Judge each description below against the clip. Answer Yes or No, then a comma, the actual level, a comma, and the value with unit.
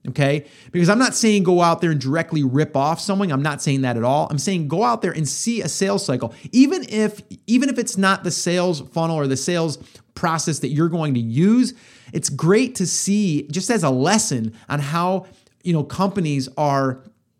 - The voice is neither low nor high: Yes, medium, 165 Hz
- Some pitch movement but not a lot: No, wide, 5.7 semitones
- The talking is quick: Yes, fast, 210 wpm